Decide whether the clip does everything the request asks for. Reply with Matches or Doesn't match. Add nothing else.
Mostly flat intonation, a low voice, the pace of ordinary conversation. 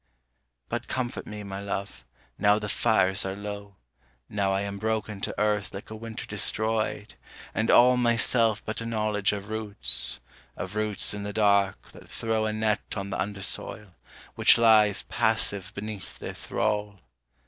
Matches